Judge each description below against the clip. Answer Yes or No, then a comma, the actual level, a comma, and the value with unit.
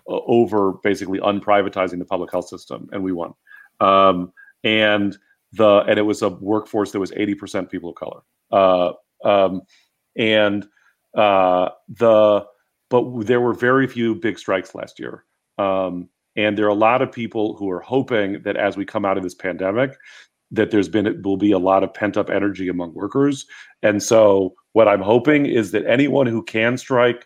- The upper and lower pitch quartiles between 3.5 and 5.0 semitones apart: No, average, 3.0 semitones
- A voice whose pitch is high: No, low, 100 Hz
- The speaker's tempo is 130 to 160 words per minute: No, average, 185 wpm